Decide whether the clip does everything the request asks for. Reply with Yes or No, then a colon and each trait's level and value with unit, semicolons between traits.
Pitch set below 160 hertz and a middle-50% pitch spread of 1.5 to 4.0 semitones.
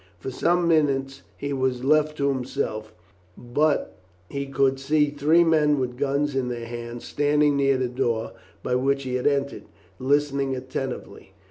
Yes: low, 135 Hz; narrow, 2.4 semitones